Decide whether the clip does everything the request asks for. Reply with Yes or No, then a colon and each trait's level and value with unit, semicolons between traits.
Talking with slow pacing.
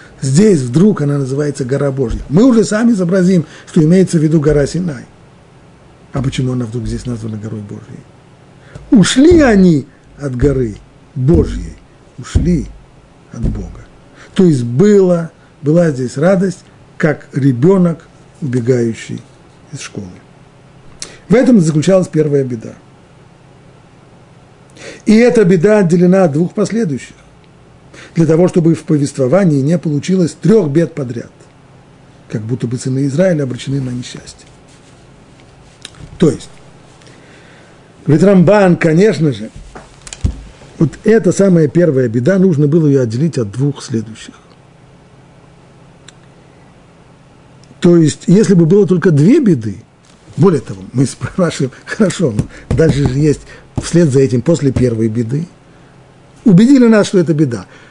No: average, 125 wpm